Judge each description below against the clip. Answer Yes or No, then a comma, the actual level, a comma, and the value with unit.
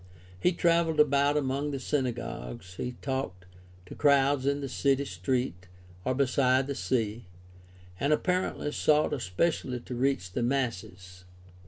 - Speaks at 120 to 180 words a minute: Yes, average, 140 wpm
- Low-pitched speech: Yes, low, 130 Hz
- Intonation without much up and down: No, average, 3.5 semitones